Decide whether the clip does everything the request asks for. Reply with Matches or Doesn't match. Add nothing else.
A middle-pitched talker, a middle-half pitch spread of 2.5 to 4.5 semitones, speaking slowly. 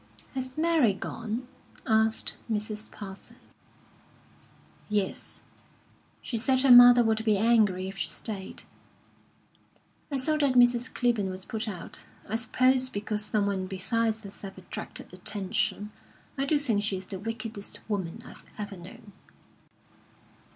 Doesn't match